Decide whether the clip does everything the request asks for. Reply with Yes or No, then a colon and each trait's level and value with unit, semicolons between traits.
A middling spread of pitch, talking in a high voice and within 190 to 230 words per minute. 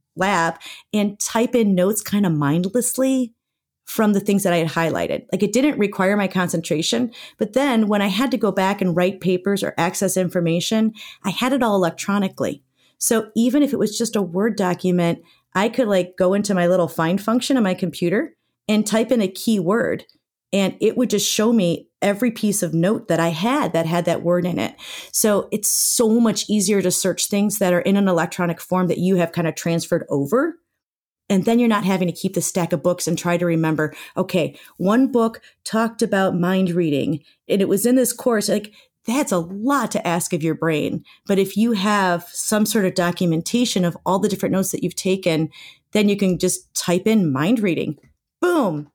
Yes: average, 4.0 semitones; high, 195 Hz; fast, 205 wpm